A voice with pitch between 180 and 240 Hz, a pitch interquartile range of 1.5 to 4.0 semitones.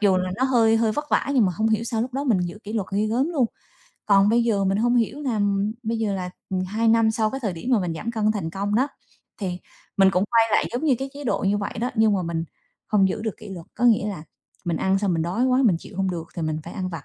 Yes: high, 210 Hz; average, 3.5 semitones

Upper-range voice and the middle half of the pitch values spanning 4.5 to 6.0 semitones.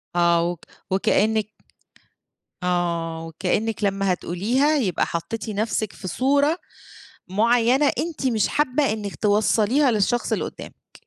Yes: high, 215 Hz; wide, 5.4 semitones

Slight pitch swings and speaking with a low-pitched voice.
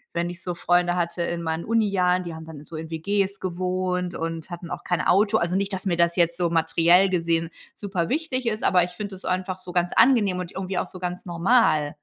No: narrow, 2.0 semitones; medium, 180 Hz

